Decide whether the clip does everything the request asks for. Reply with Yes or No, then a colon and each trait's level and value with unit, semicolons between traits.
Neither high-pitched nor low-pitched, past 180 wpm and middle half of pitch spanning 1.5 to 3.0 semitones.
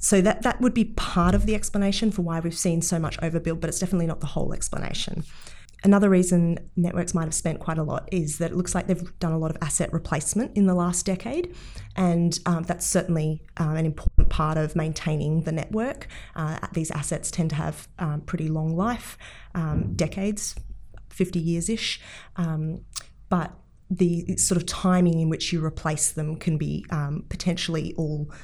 Yes: medium, 170 Hz; average, 190 wpm; narrow, 2.5 semitones